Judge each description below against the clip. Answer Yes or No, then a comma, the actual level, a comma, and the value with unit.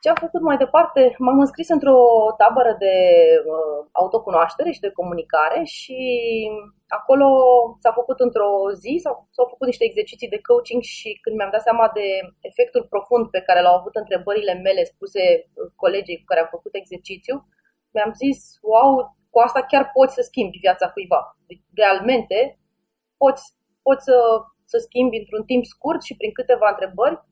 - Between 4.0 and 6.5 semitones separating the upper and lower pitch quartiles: Yes, wide, 5.4 semitones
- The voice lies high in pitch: Yes, high, 245 Hz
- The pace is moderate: Yes, average, 155 wpm